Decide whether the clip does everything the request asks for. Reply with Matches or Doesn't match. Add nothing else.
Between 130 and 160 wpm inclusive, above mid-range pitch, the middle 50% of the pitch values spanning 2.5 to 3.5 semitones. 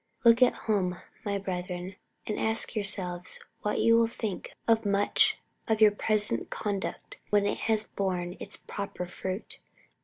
Matches